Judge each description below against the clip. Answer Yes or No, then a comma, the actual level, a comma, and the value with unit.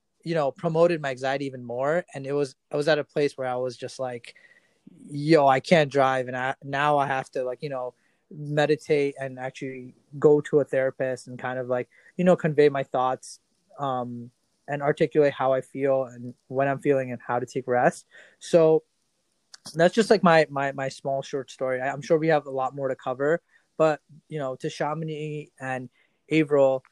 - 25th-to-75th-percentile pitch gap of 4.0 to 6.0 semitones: No, average, 2.7 semitones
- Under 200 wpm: No, fast, 205 wpm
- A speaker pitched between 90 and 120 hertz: No, medium, 140 Hz